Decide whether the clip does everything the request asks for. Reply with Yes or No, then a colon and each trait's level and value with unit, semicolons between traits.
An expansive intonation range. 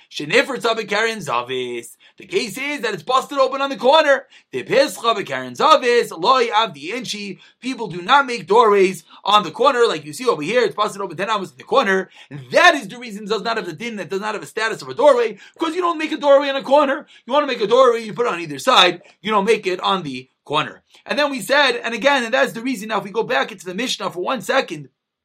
Yes: wide, 6.2 semitones